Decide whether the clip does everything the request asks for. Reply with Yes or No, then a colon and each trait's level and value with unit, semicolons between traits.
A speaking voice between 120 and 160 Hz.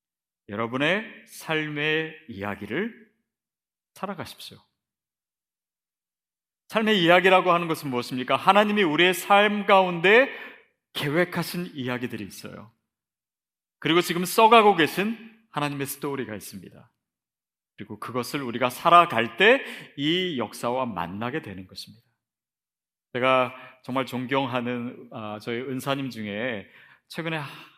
Yes: medium, 140 Hz